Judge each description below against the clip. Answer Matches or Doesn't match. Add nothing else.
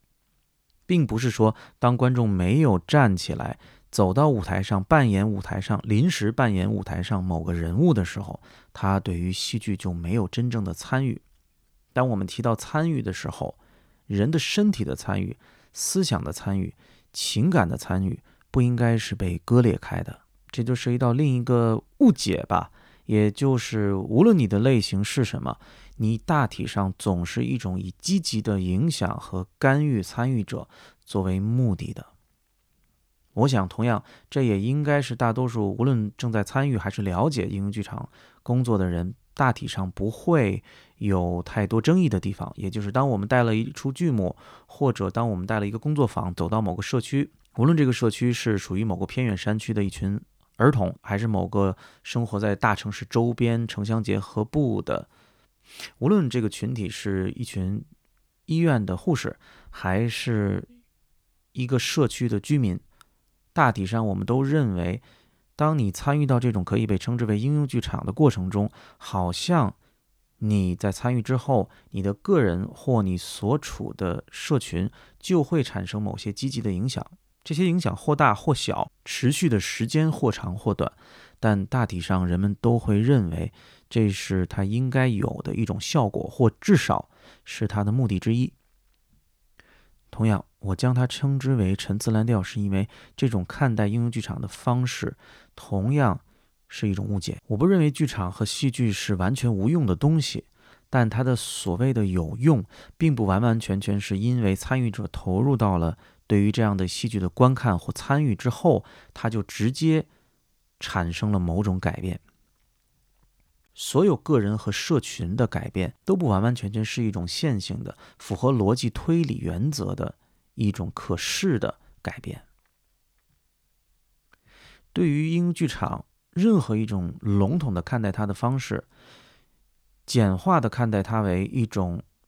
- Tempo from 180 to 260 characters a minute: Matches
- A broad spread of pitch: Doesn't match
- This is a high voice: Doesn't match